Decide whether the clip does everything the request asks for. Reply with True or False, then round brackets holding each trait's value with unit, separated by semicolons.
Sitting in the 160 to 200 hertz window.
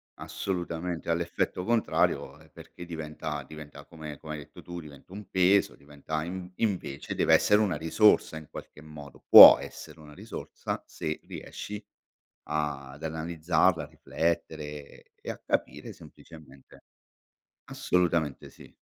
False (80 Hz)